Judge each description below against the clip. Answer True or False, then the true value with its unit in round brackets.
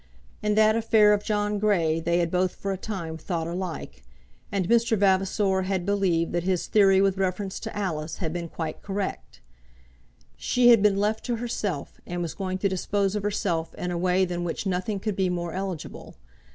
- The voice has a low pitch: False (190 Hz)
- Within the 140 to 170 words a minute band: False (190 wpm)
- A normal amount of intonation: True (3.0 semitones)